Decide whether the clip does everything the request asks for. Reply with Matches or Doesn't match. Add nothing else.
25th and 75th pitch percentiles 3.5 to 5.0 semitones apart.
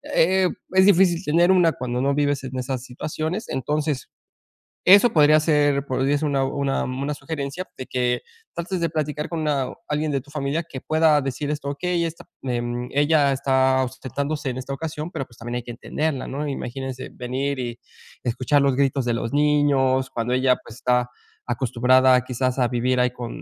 Doesn't match